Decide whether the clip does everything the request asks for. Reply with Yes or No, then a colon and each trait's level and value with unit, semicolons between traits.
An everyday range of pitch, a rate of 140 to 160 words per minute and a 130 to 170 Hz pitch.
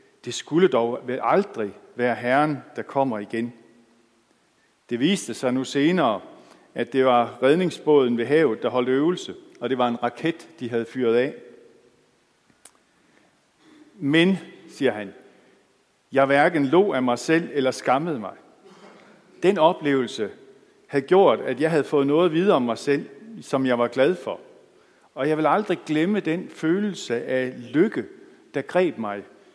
No: wide, 5.8 semitones; average, 150 wpm; medium, 140 Hz